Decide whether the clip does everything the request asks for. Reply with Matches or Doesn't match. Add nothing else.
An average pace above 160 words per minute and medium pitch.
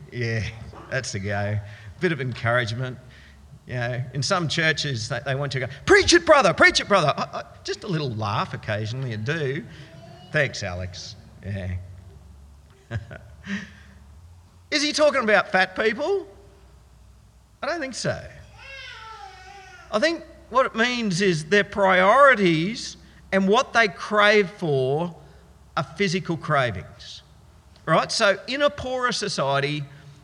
Doesn't match